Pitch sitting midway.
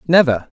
Yes: medium, 145 Hz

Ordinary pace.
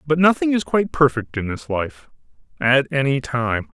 Yes: average, 175 wpm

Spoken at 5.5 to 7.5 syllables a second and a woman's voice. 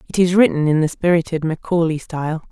Yes: 6.0 syllables/s; female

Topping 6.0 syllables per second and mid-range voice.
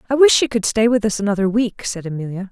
No: 6.5 syllables/s; high, 210 Hz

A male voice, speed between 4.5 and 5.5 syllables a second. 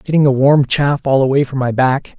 Yes: male; 5.1 syllables/s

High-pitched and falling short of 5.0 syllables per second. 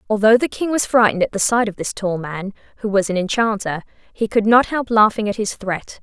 No: high, 210 Hz; 5.7 syllables/s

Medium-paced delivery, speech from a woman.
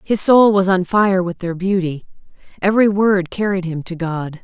Yes: average, 190 wpm; female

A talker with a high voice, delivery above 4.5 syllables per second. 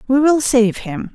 No: very high, 250 Hz; 4.1 syllables/s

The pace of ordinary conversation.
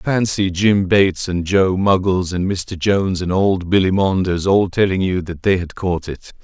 Yes: average, 195 wpm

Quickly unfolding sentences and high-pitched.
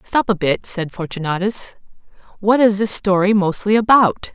No: average, 150 wpm; high, 200 Hz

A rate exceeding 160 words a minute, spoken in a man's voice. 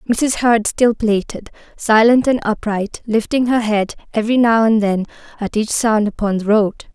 No: average, 175 wpm; female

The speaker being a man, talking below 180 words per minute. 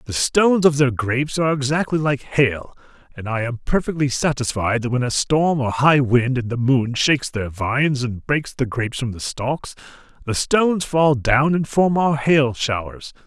No: male; average, 195 wpm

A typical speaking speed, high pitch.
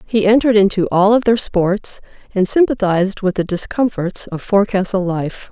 Yes: average, 165 wpm; high, 200 Hz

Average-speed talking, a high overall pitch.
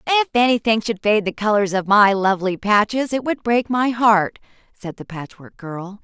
Yes: average, 190 wpm; high, 210 Hz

